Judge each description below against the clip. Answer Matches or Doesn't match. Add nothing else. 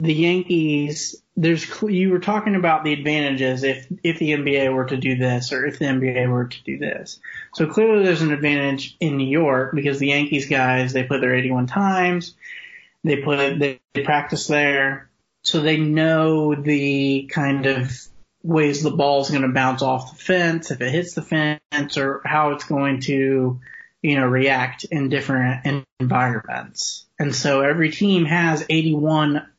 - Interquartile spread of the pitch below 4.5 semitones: Matches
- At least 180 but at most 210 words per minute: Doesn't match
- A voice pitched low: Doesn't match